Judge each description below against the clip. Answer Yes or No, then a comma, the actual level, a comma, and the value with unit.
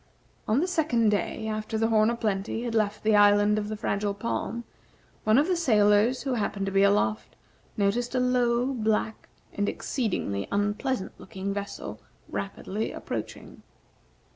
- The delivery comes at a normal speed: Yes, average, 155 wpm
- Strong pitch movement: No, average, 2.7 semitones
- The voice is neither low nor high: No, high, 215 Hz